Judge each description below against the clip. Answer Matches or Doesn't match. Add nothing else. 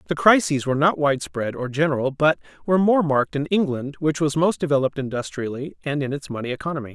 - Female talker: Doesn't match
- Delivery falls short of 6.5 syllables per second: Doesn't match